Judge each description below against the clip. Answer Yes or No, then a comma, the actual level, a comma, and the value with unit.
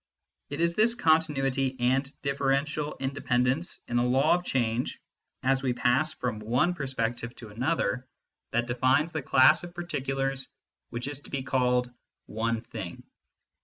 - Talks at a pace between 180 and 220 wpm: Yes, average, 185 wpm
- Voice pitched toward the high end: No, low, 135 Hz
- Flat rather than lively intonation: No, average, 3.0 semitones